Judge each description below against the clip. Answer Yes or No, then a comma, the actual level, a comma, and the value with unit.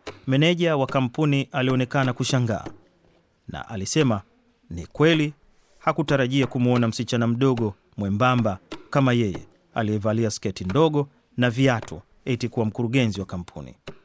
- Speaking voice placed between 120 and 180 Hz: Yes, low, 125 Hz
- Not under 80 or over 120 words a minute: Yes, average, 110 wpm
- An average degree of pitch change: Yes, average, 4.0 semitones